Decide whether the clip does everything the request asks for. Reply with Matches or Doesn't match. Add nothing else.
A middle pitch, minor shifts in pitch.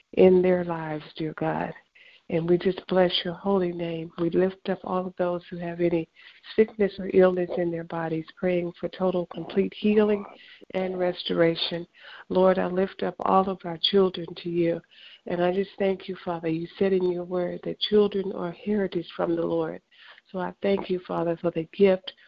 Matches